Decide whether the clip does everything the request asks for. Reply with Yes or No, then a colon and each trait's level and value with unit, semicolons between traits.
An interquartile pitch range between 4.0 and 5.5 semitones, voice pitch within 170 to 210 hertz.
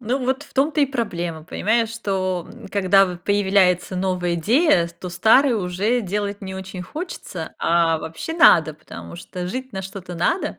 Yes: average, 4.8 semitones; high, 190 Hz